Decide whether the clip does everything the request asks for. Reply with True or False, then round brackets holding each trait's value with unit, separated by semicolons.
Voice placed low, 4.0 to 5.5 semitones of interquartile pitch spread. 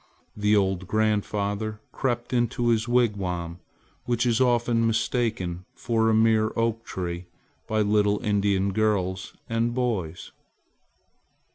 False (110 Hz; 2.8 semitones)